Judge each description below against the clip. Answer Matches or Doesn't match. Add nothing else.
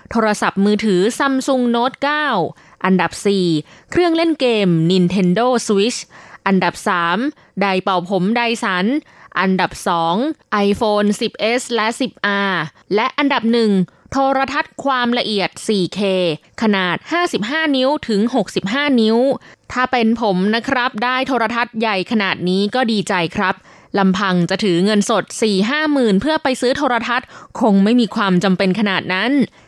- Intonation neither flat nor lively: Matches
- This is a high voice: Matches